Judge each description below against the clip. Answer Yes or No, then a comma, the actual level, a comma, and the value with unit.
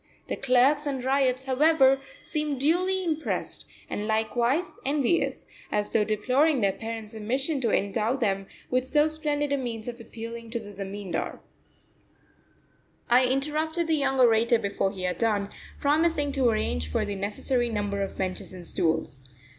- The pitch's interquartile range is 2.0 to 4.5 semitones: No, average, 5.3 semitones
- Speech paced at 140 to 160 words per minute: Yes, average, 155 wpm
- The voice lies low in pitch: No, high, 245 Hz